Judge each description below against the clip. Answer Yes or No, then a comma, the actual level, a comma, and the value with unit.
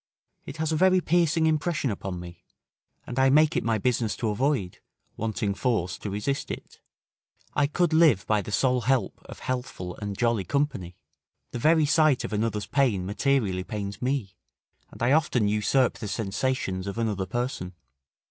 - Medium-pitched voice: No, low, 120 Hz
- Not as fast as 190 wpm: Yes, average, 165 wpm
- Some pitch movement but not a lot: No, wide, 5.8 semitones